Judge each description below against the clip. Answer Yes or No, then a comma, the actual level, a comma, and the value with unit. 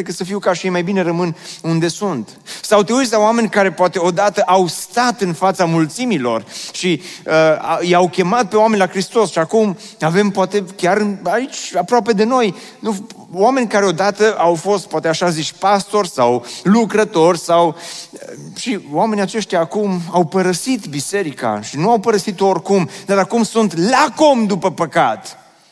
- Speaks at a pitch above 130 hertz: Yes, high, 190 Hz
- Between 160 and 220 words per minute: Yes, fast, 170 wpm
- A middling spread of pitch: Yes, average, 3.8 semitones